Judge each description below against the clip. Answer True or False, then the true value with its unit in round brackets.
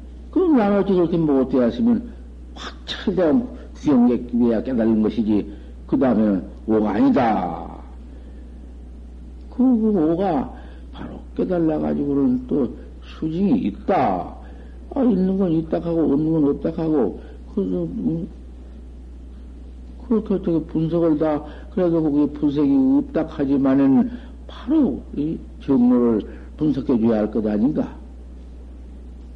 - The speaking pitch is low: True (120 Hz)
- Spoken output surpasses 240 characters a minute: False (235 characters per minute)